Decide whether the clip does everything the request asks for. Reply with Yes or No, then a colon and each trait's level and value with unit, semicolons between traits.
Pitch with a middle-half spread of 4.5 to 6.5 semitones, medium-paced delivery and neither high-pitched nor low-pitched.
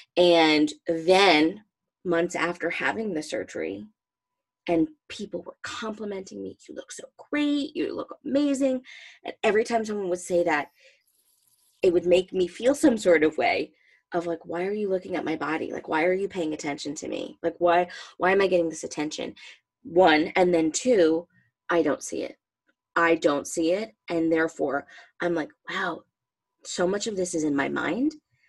Yes: average, 4.8 semitones; average, 180 wpm; medium, 175 Hz